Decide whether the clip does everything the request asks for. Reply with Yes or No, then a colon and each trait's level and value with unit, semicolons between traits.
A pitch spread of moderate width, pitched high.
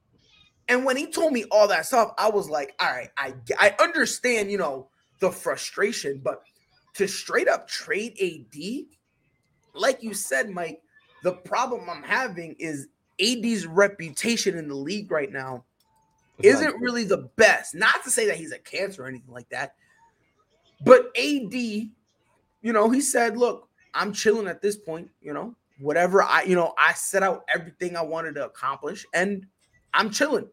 No: wide, 6.7 semitones; high, 200 Hz